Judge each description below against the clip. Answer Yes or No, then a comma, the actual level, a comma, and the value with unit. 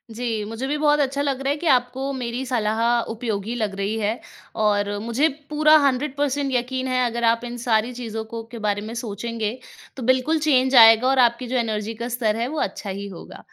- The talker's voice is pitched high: Yes, high, 240 Hz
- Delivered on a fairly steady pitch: No, average, 3.2 semitones